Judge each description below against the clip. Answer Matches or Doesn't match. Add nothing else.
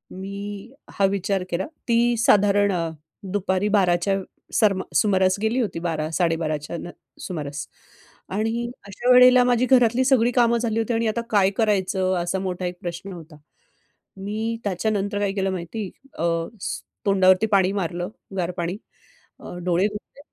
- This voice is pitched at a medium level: Doesn't match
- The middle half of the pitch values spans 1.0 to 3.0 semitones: Doesn't match